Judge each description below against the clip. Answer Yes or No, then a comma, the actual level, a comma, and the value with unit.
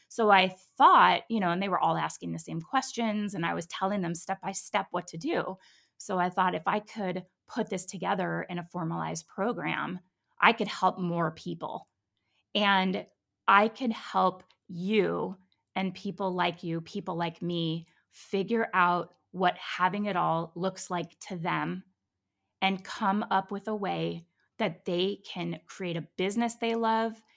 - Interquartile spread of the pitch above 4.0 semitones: No, narrow, 2.6 semitones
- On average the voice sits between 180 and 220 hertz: Yes, medium, 185 Hz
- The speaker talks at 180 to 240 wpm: No, average, 170 wpm